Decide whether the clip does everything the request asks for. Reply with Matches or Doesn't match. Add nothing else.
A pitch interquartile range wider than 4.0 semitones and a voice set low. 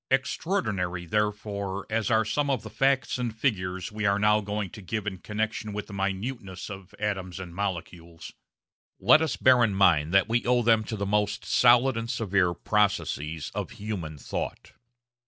Doesn't match